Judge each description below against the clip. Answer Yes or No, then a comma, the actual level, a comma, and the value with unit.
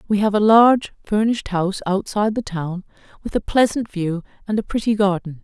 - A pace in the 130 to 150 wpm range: No, average, 190 wpm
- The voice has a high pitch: Yes, high, 200 Hz